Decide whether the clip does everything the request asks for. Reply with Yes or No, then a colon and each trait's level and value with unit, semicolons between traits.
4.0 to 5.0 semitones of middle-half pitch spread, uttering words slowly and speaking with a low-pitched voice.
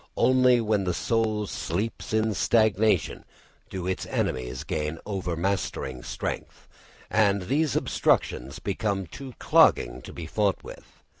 Yes: average, 4.4 semitones; slow, 125 wpm; low, 100 Hz